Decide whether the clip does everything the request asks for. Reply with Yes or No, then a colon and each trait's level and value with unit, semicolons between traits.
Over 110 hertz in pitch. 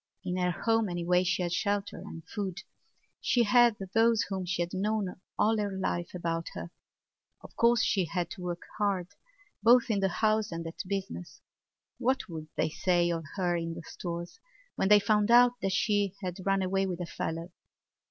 Yes: high, 190 Hz